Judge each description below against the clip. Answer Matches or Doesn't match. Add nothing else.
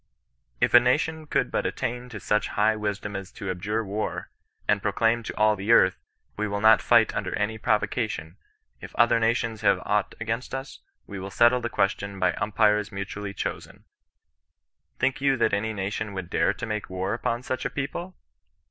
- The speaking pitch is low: Matches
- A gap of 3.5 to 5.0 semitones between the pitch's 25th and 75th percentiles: Doesn't match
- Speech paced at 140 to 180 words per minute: Doesn't match